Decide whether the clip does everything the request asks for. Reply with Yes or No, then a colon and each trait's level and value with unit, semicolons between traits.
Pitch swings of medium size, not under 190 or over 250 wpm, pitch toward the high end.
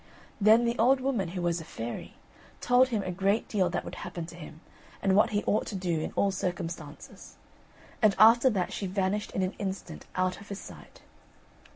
Yes: average, 3.5 semitones; average, 200 wpm; high, 195 Hz